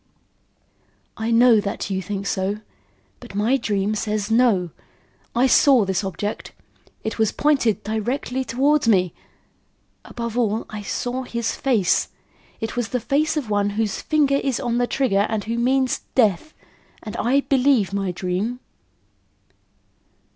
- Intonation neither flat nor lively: Yes, average, 3.8 semitones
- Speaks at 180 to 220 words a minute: No, average, 140 wpm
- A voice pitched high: Yes, high, 225 Hz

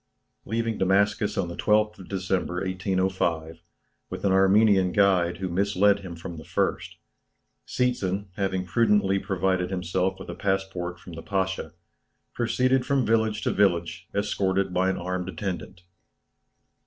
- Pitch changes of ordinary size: No, narrow, 2.1 semitones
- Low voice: Yes, very low, 95 Hz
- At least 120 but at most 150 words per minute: Yes, average, 140 wpm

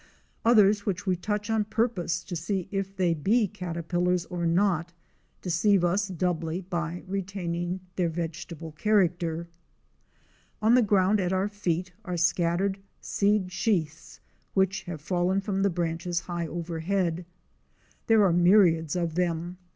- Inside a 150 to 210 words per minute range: No, slow, 135 wpm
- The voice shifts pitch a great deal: No, narrow, 2.6 semitones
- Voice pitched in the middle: Yes, medium, 180 Hz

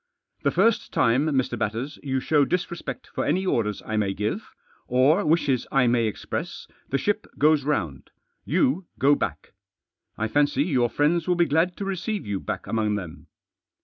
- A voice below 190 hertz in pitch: Yes, medium, 140 Hz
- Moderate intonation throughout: No, wide, 6.5 semitones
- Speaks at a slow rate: No, average, 175 wpm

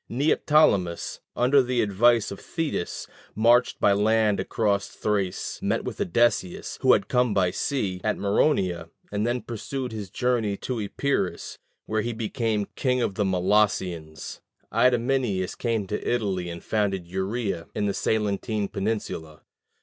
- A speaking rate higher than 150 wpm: No, average, 140 wpm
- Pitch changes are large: No, average, 3.8 semitones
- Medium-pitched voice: No, low, 105 Hz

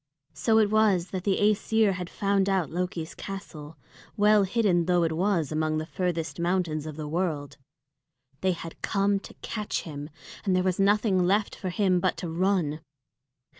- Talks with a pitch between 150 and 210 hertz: Yes, medium, 185 Hz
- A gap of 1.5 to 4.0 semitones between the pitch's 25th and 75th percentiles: Yes, average, 3.4 semitones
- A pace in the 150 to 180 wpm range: Yes, average, 170 wpm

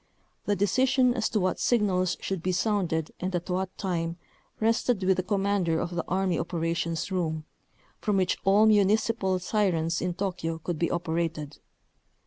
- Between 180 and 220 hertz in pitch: Yes, medium, 185 Hz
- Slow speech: No, average, 155 wpm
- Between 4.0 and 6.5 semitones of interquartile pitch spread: No, average, 3.2 semitones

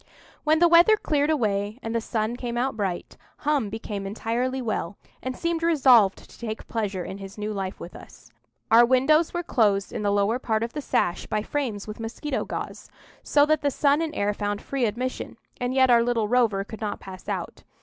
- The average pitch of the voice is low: No, high, 230 Hz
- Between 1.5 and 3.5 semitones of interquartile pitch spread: No, average, 4.7 semitones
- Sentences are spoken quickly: Yes, fast, 210 wpm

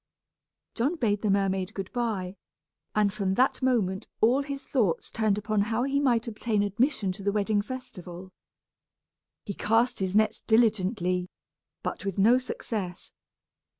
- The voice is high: Yes, high, 210 Hz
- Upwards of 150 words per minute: No, average, 145 wpm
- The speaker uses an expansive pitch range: No, average, 3.6 semitones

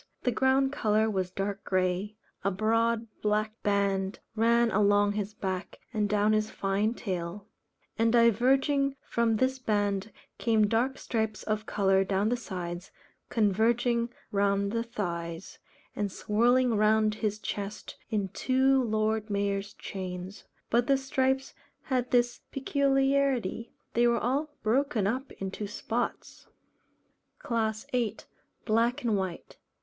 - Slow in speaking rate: Yes, slow, 130 wpm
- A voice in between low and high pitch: No, high, 215 Hz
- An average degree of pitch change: Yes, average, 3.1 semitones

